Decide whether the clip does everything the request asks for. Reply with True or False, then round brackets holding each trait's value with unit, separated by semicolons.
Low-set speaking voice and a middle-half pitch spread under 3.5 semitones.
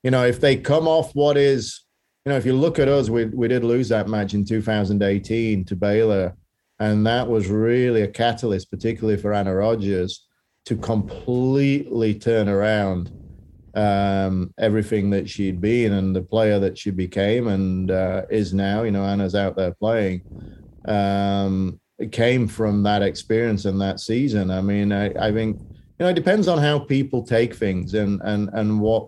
True (105 Hz; 2.9 semitones)